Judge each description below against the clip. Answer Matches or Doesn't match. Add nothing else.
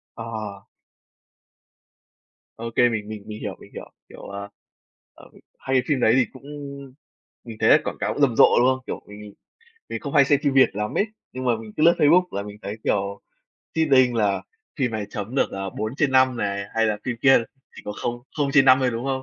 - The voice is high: Doesn't match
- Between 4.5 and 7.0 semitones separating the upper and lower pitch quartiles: Doesn't match